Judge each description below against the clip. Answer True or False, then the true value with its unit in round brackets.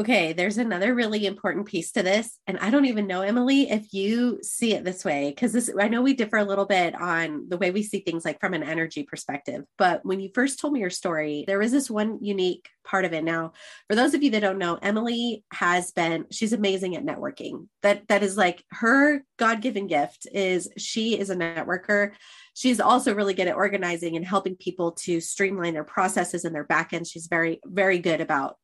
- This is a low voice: False (195 Hz)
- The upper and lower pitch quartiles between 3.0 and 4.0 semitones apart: True (3.7 semitones)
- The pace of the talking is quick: True (215 wpm)